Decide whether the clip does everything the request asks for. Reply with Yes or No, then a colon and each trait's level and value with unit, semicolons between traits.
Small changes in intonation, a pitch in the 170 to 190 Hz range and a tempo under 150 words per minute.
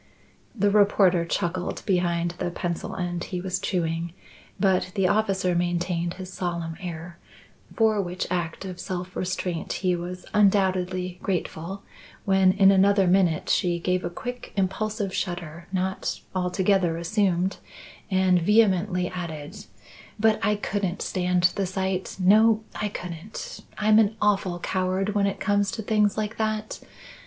Yes: narrow, 2.3 semitones; medium, 185 Hz; average, 140 wpm